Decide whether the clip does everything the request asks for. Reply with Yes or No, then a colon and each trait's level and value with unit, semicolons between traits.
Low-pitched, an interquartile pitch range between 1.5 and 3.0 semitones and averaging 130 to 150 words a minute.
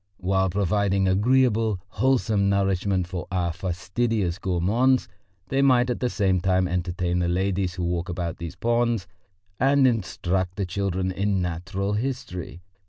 No: very low, 95 Hz; average, 3.8 semitones; average, 140 wpm